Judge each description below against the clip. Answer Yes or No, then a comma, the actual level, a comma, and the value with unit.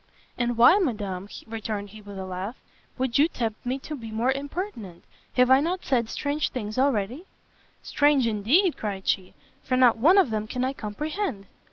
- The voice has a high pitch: Yes, high, 240 Hz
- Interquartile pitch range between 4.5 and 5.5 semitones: Yes, average, 5.2 semitones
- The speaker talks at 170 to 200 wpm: Yes, average, 180 wpm